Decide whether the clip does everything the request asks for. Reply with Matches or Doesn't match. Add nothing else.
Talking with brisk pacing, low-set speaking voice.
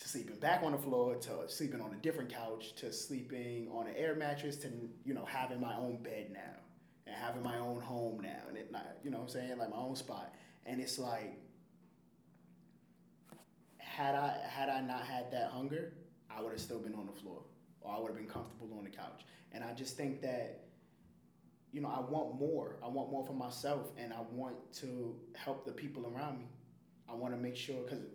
Matches